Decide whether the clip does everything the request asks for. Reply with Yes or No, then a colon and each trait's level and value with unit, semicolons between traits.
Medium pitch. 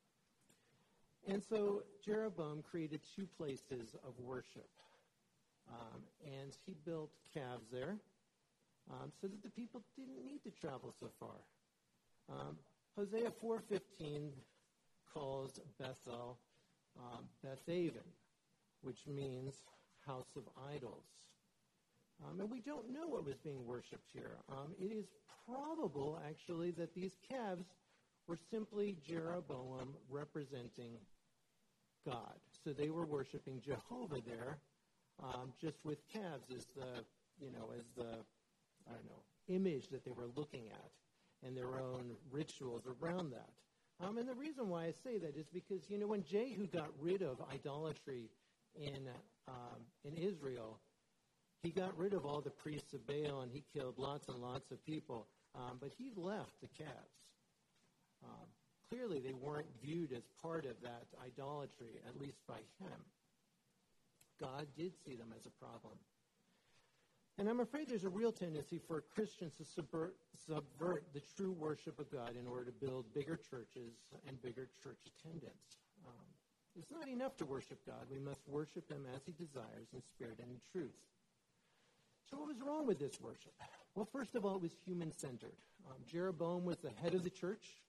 Yes: medium, 150 Hz